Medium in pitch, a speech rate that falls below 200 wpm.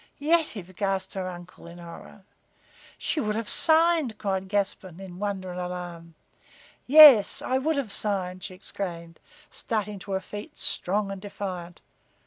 No: high, 195 Hz; average, 145 wpm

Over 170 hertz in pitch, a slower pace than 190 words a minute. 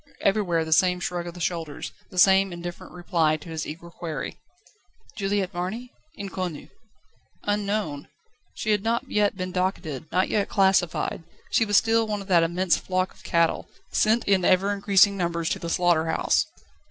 Yes: medium, 185 Hz; average, 165 wpm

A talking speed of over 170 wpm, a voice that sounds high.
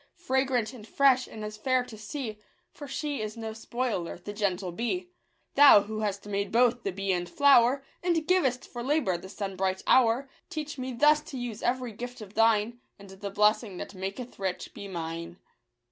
Yes: average, 185 wpm; high, 225 Hz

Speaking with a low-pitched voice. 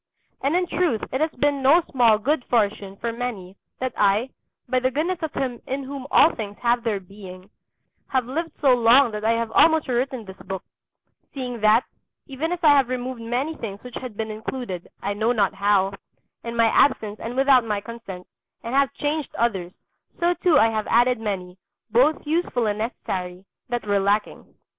No: high, 235 Hz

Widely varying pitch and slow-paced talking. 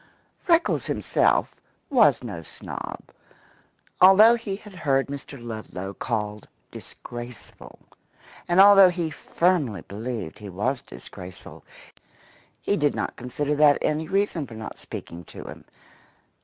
Yes: wide, 8.9 semitones; slow, 120 wpm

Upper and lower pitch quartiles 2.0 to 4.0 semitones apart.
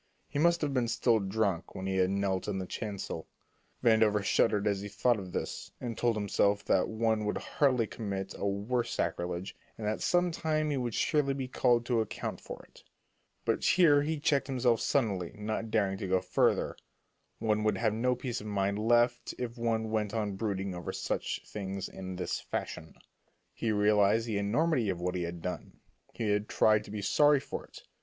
Yes: average, 3.5 semitones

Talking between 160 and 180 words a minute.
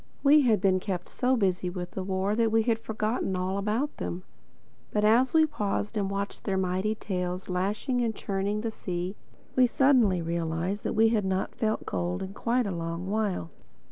No: average, 190 wpm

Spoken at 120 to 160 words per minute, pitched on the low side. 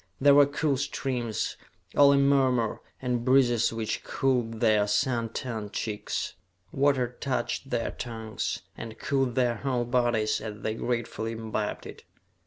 Yes: average, 140 wpm; low, 120 Hz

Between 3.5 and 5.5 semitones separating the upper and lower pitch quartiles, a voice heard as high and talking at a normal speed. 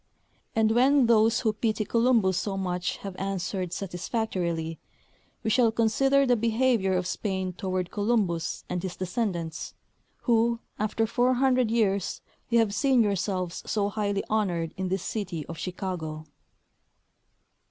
No: average, 4.0 semitones; high, 205 Hz; slow, 130 wpm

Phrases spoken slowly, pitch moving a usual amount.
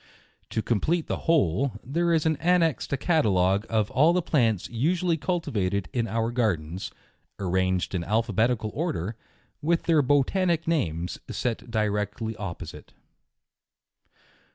No: slow, 125 wpm; wide, 8.0 semitones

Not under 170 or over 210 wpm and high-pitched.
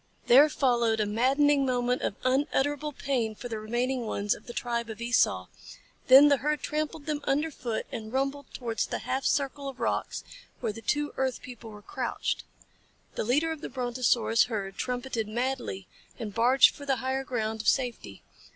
Yes: average, 175 wpm; very high, 250 Hz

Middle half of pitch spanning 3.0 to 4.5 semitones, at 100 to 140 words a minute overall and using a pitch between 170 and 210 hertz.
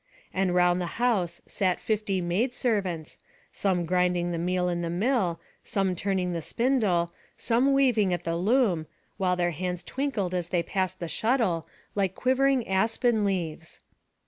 No: average, 4.2 semitones; average, 155 wpm; medium, 185 Hz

